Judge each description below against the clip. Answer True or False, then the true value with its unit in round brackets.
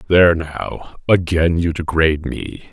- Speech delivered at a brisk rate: False (130 wpm)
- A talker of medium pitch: False (85 Hz)